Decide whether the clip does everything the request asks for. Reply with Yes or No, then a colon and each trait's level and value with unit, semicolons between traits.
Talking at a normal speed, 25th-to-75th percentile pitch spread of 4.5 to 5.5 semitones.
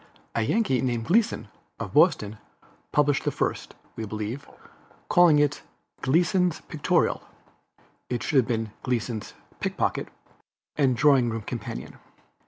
No: slow, 120 wpm; average, 4.8 semitones